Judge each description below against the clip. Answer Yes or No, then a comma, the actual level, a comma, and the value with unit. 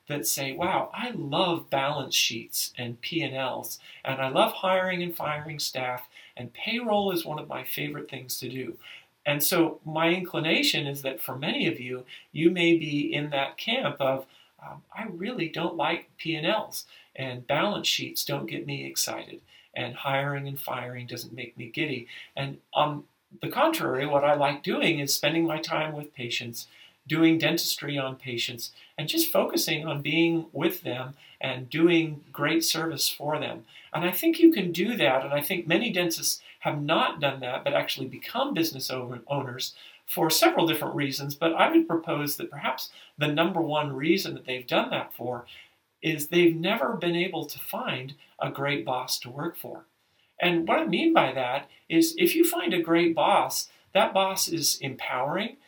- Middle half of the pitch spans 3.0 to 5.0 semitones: Yes, average, 4.0 semitones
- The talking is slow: No, average, 180 wpm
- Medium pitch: Yes, medium, 155 Hz